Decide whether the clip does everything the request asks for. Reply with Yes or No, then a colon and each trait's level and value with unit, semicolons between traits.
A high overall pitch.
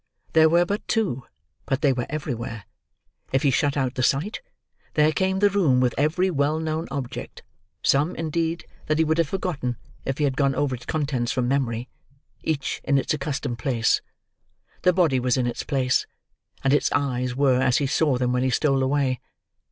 No: medium, 140 Hz